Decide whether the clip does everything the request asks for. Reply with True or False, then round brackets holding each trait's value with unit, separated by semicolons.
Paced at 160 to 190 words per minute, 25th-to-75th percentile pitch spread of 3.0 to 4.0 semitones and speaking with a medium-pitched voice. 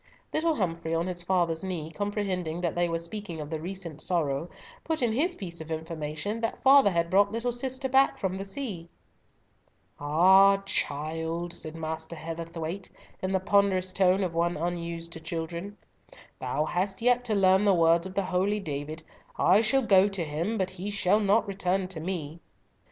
True (180 wpm; 3.4 semitones; 180 Hz)